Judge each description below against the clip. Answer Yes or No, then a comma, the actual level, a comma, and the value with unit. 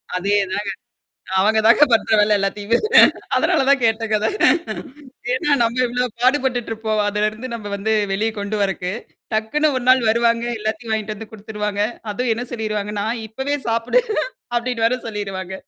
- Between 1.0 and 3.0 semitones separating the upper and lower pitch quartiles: Yes, narrow, 2.4 semitones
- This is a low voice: No, high, 220 Hz